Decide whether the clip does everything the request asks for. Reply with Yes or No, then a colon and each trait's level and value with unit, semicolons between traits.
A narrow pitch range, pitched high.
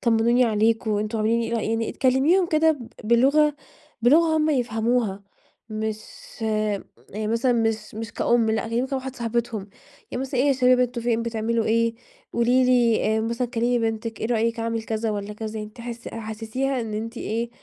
Yes: narrow, 2.1 semitones; high, 230 Hz